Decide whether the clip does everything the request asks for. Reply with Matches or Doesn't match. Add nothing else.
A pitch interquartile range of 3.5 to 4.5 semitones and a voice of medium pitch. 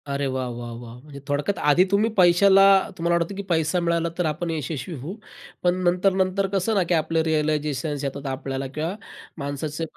Matches